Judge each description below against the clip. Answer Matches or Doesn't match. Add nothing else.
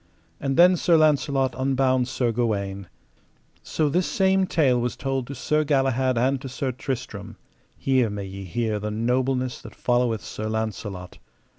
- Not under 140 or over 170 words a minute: Matches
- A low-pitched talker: Matches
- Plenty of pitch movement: Doesn't match